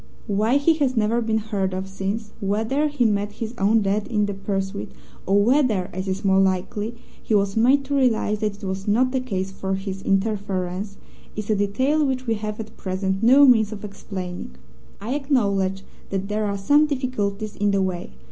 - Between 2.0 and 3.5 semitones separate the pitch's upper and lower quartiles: Yes, average, 3.2 semitones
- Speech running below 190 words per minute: No, average, 195 wpm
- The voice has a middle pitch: No, high, 210 Hz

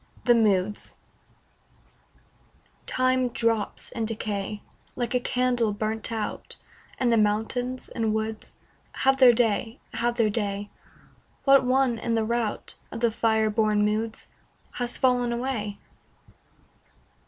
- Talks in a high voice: Yes, high, 230 Hz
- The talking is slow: Yes, slow, 120 wpm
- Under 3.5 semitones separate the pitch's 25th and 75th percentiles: Yes, narrow, 2.4 semitones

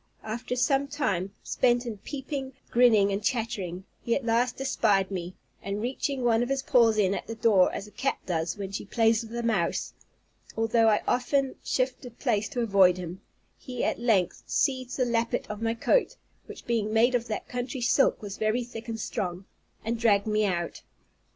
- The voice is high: Yes, high, 225 Hz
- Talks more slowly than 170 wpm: No, average, 190 wpm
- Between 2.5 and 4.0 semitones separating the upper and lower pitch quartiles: Yes, average, 3.4 semitones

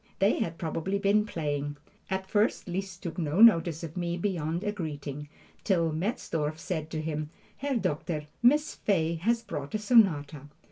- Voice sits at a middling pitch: Yes, medium, 170 Hz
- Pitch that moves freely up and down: No, average, 4.7 semitones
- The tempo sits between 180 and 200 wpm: No, average, 160 wpm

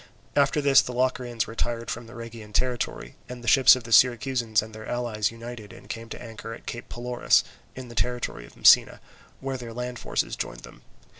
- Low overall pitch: Yes, low, 120 Hz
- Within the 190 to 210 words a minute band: Yes, average, 200 wpm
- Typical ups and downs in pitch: No, narrow, 1.7 semitones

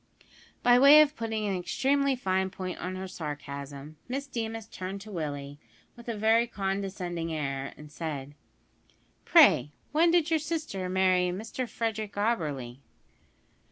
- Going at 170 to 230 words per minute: No, average, 140 wpm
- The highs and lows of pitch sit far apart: Yes, wide, 6.9 semitones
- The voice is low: No, high, 190 Hz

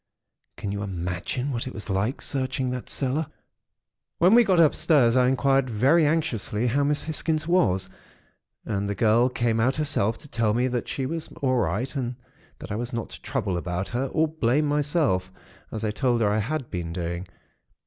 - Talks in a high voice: No, low, 125 Hz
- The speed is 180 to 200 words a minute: Yes, average, 190 wpm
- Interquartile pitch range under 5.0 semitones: No, wide, 5.4 semitones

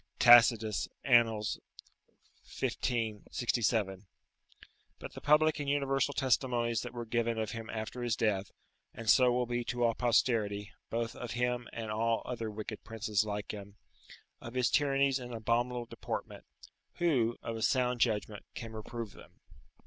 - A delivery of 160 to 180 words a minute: No, average, 150 wpm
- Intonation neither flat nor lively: No, narrow, 2.1 semitones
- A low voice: Yes, low, 115 Hz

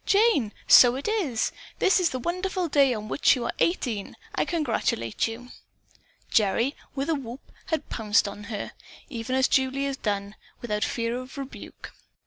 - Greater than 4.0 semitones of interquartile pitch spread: Yes, average, 5.0 semitones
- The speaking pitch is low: No, very high, 255 Hz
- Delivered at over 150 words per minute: Yes, average, 165 wpm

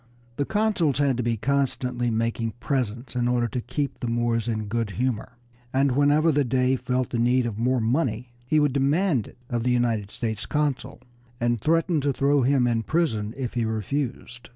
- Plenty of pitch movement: No, average, 3.1 semitones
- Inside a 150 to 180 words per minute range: No, average, 195 wpm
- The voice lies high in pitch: No, low, 125 Hz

